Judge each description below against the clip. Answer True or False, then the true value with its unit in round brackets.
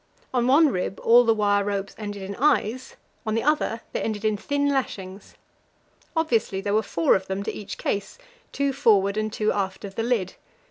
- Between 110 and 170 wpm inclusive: False (195 wpm)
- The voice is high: True (215 Hz)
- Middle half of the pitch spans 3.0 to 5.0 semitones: True (3.6 semitones)